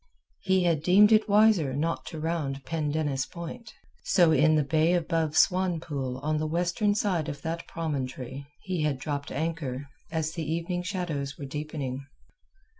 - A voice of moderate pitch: Yes, medium, 160 Hz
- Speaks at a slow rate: No, average, 155 wpm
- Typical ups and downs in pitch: Yes, average, 3.4 semitones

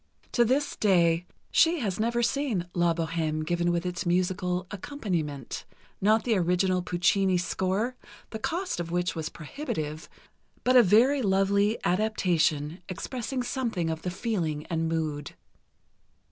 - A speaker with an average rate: No, slow, 130 wpm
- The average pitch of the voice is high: No, medium, 180 Hz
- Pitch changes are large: No, average, 4.8 semitones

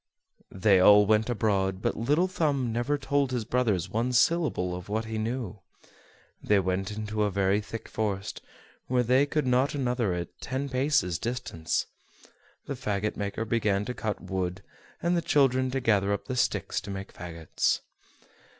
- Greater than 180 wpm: No, average, 170 wpm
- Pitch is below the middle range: Yes, low, 110 Hz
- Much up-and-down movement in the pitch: No, average, 4.5 semitones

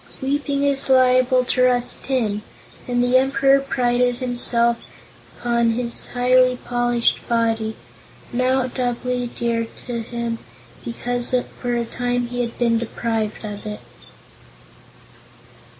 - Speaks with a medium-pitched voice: No, high, 245 Hz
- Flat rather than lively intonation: Yes, narrow, 1.3 semitones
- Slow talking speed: Yes, slow, 120 wpm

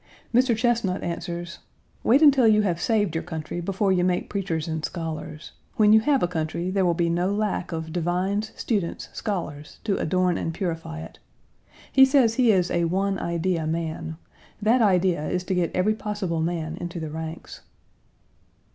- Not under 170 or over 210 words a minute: Yes, average, 175 wpm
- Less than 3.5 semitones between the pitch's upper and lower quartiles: No, average, 4.1 semitones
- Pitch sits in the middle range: Yes, medium, 180 Hz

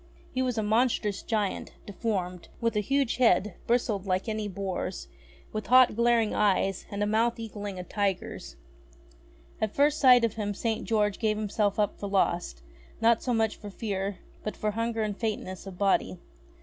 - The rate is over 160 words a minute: Yes, average, 175 wpm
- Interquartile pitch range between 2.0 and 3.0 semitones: Yes, narrow, 2.5 semitones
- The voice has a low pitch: No, high, 210 Hz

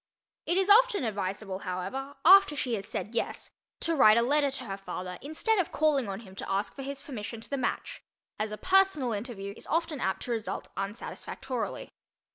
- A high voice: Yes, high, 245 Hz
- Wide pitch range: Yes, wide, 7.2 semitones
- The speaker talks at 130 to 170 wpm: No, average, 195 wpm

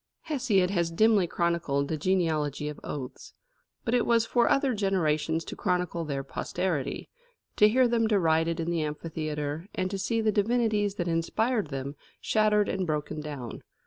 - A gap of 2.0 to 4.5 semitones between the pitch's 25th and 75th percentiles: No, wide, 5.6 semitones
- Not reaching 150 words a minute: No, average, 160 wpm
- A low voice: No, medium, 175 Hz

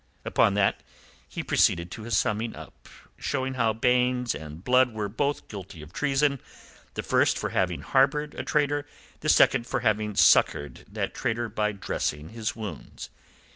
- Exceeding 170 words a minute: No, average, 160 wpm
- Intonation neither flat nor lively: Yes, average, 4.3 semitones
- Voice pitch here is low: Yes, low, 115 Hz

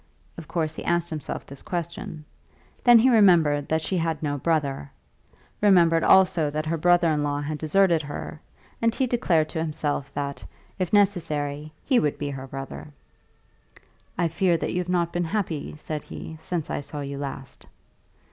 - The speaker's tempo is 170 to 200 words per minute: Yes, average, 175 wpm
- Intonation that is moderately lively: Yes, average, 3.2 semitones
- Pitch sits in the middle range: Yes, medium, 160 Hz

